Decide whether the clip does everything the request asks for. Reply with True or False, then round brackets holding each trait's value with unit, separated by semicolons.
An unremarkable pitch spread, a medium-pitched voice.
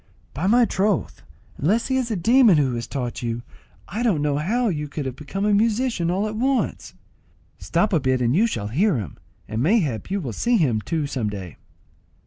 False (8.8 semitones; 170 Hz)